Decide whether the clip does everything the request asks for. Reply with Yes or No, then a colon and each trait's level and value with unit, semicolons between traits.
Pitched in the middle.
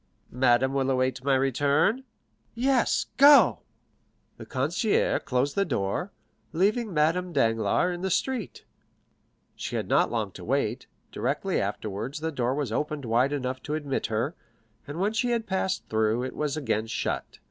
Yes: medium, 145 Hz